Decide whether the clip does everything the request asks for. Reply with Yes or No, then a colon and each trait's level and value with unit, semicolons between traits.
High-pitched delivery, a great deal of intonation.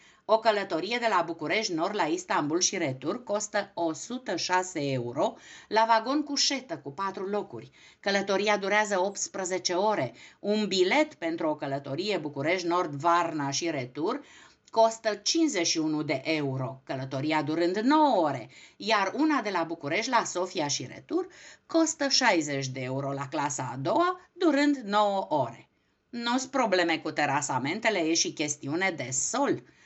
Yes: high, 195 Hz; wide, 7.1 semitones